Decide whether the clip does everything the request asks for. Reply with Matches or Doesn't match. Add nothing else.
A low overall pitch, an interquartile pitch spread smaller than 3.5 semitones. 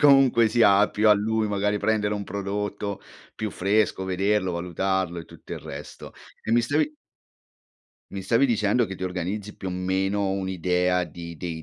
Matches